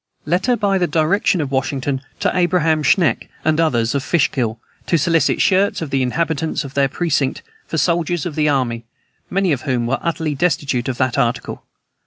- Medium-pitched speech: Yes, medium, 150 Hz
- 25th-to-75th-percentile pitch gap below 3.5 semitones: No, average, 4.4 semitones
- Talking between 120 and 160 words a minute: No, average, 185 wpm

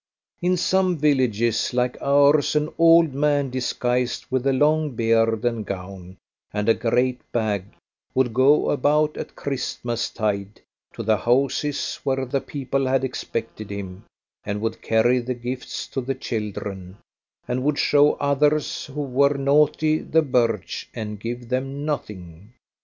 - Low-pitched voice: Yes, low, 125 Hz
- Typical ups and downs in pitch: Yes, average, 4.1 semitones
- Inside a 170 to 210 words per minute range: No, average, 140 wpm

